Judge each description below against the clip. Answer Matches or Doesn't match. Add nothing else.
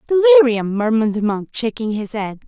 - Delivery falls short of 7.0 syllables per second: Doesn't match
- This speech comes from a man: Doesn't match